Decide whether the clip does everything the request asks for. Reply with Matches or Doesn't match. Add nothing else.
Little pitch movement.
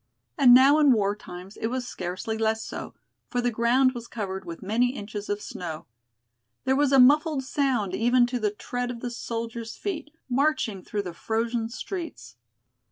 Doesn't match